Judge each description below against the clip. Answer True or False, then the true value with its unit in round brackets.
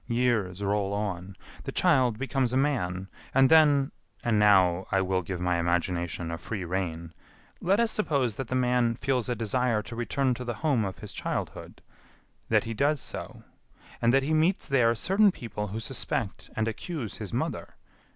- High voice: False (115 Hz)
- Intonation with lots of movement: True (5.7 semitones)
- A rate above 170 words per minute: True (180 wpm)